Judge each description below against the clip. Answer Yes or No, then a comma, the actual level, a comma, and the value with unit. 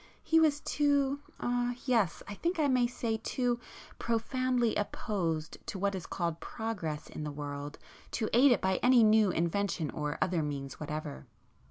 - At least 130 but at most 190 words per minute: Yes, average, 165 wpm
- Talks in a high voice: Yes, high, 215 Hz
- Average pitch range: No, wide, 7.3 semitones